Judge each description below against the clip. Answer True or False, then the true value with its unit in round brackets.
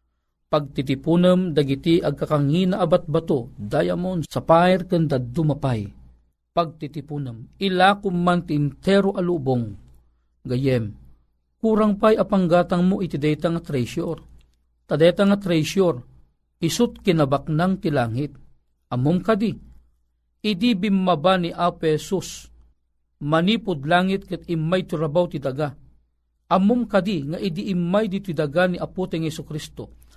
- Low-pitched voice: False (160 Hz)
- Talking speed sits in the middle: False (95 wpm)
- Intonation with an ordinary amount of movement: False (6.5 semitones)